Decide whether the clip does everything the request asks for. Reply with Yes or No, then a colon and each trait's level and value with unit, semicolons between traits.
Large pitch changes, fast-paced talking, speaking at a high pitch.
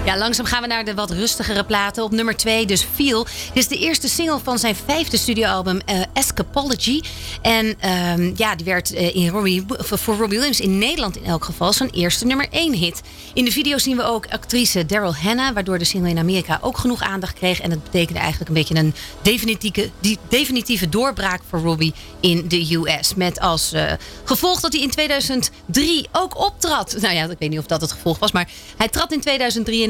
Yes: wide, 5.9 semitones; fast, 210 wpm; high, 220 Hz